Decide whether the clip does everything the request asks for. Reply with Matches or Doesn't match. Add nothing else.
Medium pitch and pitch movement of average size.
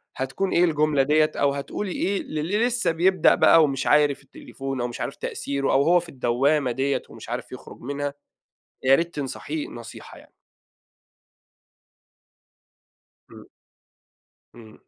Matches